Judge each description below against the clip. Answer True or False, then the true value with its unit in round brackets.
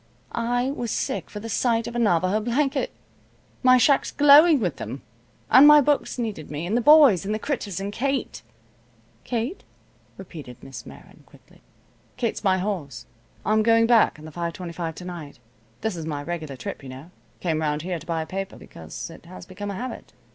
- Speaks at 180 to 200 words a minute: True (190 wpm)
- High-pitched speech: True (200 Hz)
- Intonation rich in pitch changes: True (6.7 semitones)